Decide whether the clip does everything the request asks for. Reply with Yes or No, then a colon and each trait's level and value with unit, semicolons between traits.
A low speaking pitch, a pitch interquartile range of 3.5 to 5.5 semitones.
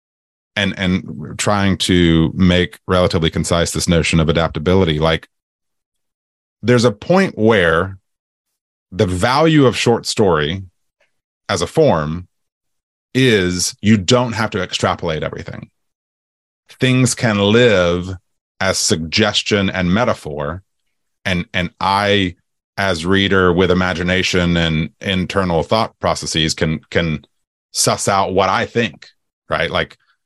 Yes: very low, 90 Hz; average, 3.8 semitones